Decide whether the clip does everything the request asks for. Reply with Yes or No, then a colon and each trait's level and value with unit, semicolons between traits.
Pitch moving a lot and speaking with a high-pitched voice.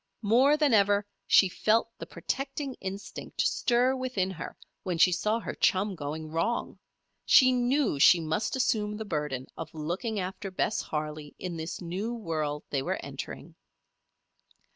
Yes: wide, 6.3 semitones; high, 195 Hz